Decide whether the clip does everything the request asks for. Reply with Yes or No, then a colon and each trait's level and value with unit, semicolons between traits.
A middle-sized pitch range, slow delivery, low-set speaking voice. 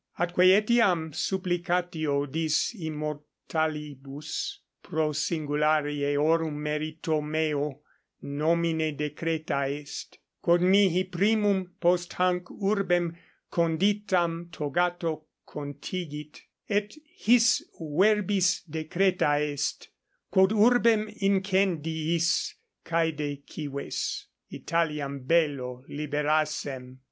No: average, 3.4 semitones; slow, 75 wpm; medium, 160 Hz